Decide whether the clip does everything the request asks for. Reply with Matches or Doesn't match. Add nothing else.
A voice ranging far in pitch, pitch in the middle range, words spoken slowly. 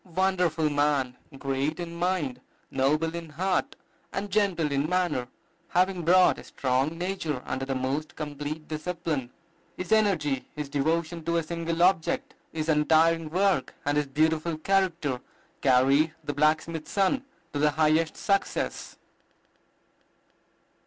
Doesn't match